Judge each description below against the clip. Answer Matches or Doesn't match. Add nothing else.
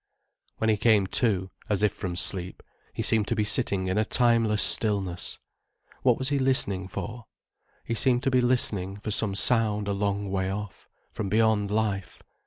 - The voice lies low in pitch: Matches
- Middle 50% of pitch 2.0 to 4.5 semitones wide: Matches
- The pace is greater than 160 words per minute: Matches